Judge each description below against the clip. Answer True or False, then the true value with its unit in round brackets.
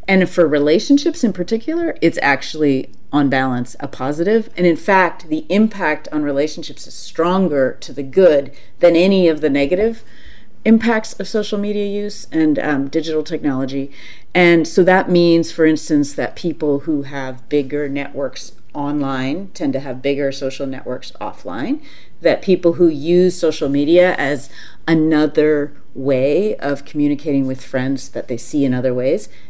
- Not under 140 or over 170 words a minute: True (155 wpm)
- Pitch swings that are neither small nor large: True (4.7 semitones)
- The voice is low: False (155 Hz)